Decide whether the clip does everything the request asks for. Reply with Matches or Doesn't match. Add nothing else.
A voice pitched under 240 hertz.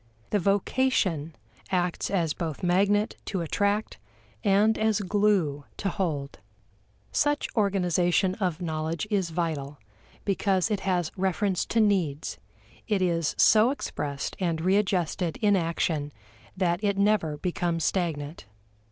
Matches